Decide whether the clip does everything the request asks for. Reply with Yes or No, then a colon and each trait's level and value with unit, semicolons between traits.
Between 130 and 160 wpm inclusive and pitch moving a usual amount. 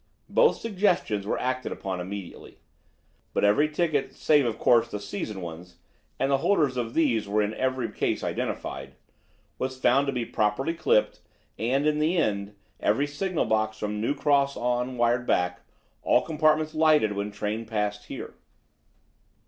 No: average, 155 wpm; wide, 5.8 semitones